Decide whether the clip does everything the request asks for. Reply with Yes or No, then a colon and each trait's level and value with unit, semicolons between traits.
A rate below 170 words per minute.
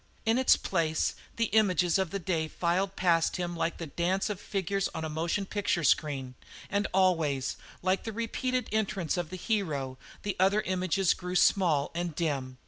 No: average, 175 wpm